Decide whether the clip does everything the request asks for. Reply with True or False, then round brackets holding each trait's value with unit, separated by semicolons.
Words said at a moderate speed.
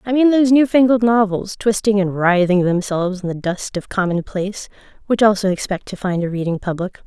True (195 wpm)